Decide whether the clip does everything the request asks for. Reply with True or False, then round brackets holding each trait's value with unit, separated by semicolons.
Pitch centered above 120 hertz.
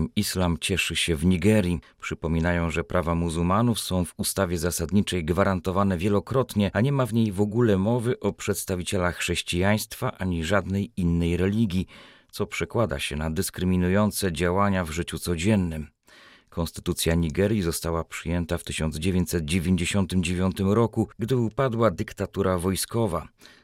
False (95 Hz)